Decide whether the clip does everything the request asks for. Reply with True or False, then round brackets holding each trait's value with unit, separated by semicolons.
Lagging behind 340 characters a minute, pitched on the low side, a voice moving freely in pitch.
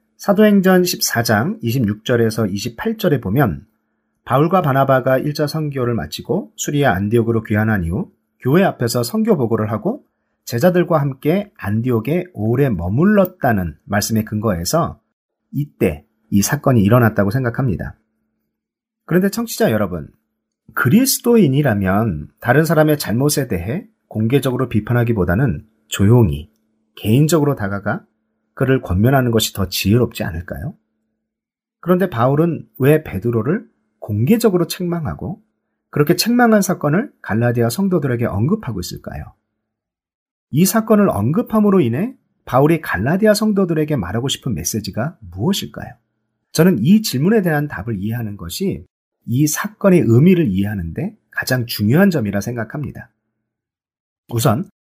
True (310 characters per minute; 125 Hz; 7.8 semitones)